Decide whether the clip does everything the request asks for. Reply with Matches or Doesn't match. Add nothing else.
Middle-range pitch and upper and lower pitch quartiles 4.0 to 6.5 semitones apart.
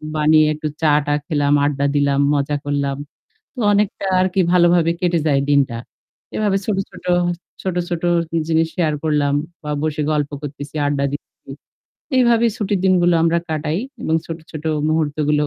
Doesn't match